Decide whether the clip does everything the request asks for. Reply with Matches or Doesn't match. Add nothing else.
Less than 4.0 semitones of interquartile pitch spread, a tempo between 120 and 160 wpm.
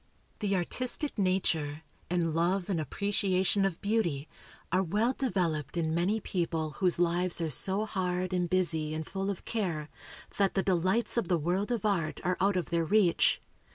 Doesn't match